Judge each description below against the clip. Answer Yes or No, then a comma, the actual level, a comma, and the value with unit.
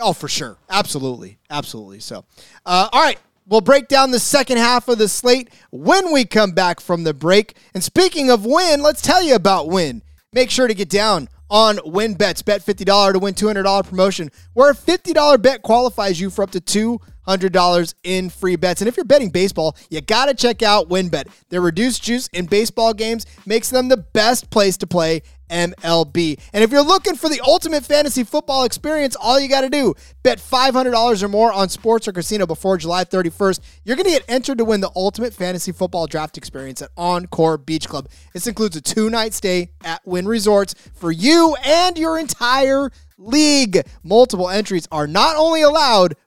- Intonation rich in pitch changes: Yes, wide, 6.0 semitones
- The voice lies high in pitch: Yes, high, 210 Hz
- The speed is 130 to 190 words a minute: No, average, 200 wpm